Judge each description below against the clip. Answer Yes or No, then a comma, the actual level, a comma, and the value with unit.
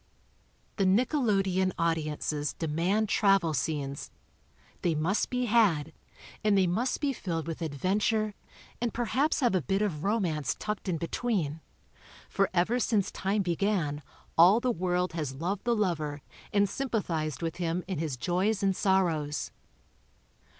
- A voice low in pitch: No, medium, 185 Hz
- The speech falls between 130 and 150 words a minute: Yes, average, 145 wpm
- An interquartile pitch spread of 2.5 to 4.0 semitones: No, average, 4.7 semitones